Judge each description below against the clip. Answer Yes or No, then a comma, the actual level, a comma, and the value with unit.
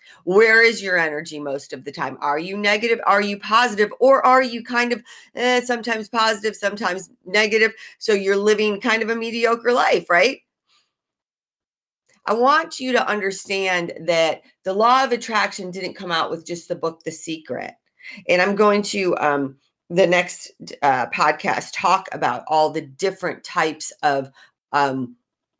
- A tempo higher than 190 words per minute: No, average, 160 wpm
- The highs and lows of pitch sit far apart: Yes, wide, 5.7 semitones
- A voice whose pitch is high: Yes, high, 200 Hz